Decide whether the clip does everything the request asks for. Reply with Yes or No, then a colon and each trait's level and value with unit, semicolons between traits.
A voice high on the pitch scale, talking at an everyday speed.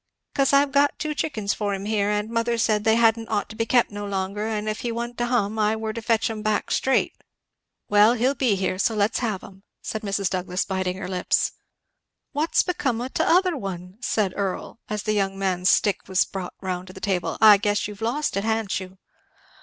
No: high, 210 Hz; fast, 215 wpm